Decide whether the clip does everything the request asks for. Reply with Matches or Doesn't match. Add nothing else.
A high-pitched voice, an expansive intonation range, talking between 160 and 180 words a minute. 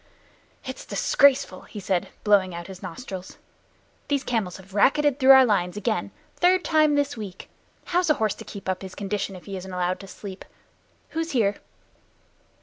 Matches